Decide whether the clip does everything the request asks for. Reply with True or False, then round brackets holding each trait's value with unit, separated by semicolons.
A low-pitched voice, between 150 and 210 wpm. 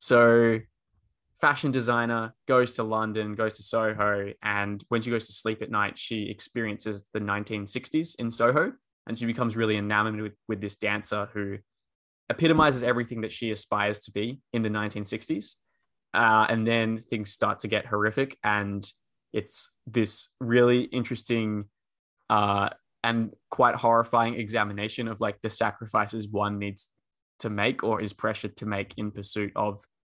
True (110 Hz; 155 wpm)